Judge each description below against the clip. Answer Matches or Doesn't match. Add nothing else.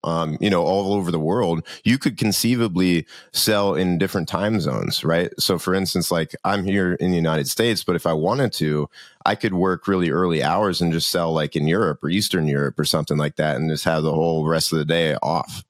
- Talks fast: Matches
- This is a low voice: Matches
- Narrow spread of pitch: Doesn't match